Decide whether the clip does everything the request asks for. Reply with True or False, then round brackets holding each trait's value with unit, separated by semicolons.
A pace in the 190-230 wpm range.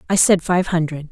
True (215 wpm)